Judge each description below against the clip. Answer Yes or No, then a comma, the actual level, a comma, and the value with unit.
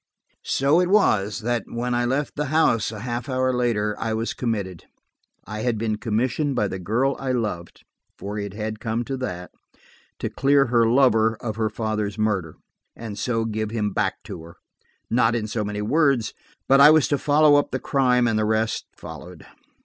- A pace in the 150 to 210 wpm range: Yes, average, 180 wpm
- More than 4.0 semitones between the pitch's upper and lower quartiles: No, average, 3.4 semitones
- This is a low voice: Yes, low, 115 Hz